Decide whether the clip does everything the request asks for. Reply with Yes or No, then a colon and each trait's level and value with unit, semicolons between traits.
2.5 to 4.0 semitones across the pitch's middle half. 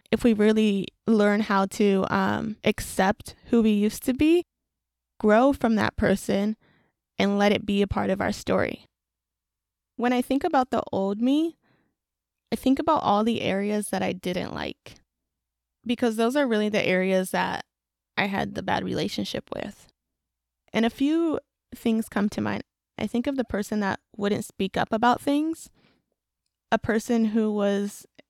Yes: average, 3.7 semitones